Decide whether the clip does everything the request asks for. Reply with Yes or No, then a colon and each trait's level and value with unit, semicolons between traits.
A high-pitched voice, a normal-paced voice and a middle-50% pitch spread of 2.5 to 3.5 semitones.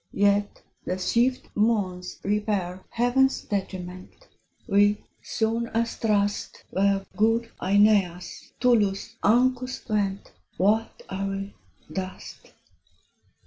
No: high, 205 Hz; slow, 95 wpm; average, 2.9 semitones